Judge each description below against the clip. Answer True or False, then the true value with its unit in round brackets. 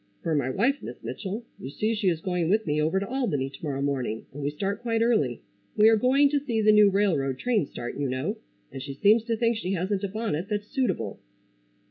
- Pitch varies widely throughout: True (7.5 semitones)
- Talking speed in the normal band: False (230 wpm)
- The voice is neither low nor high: False (195 Hz)